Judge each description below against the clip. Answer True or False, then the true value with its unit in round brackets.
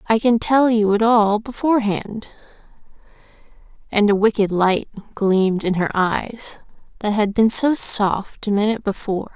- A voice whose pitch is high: True (215 Hz)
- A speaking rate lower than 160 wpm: True (150 wpm)